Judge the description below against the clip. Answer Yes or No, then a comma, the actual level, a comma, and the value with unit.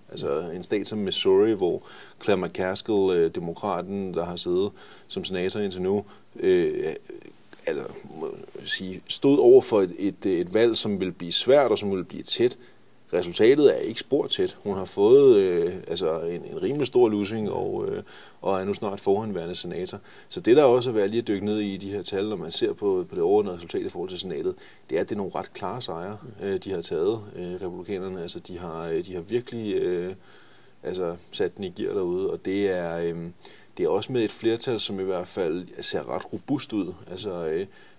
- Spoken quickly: No, average, 210 wpm